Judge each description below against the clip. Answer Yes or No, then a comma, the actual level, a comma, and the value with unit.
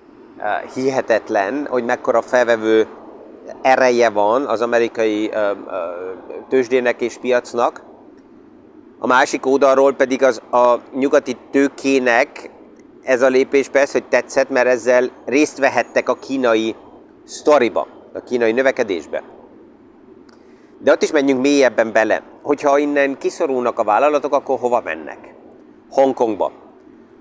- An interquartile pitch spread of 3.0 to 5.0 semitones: No, narrow, 2.6 semitones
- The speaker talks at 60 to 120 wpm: Yes, average, 110 wpm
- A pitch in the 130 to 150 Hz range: Yes, low, 135 Hz